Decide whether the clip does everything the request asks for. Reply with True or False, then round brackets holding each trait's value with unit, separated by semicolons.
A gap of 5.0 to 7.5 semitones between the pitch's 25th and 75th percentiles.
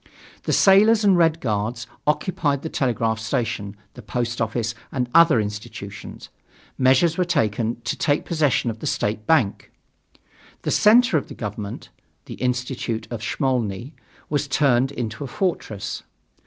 True (5.5 semitones)